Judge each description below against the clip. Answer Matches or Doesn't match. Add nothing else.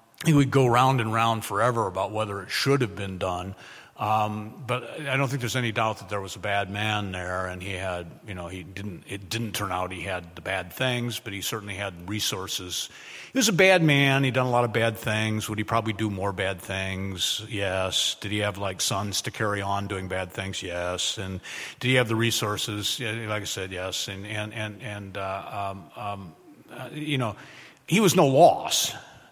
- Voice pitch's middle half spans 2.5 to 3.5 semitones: Matches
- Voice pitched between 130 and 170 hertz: Doesn't match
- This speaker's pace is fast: Matches